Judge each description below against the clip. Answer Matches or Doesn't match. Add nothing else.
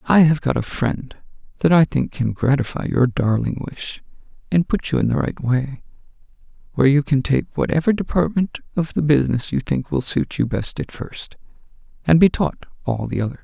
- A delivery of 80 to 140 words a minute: Doesn't match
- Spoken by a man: Matches